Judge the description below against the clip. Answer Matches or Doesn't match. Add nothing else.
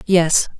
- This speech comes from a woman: Matches